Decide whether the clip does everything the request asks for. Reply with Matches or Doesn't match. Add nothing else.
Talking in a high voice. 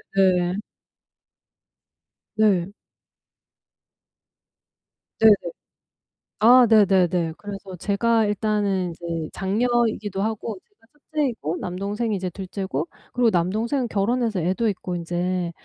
Matches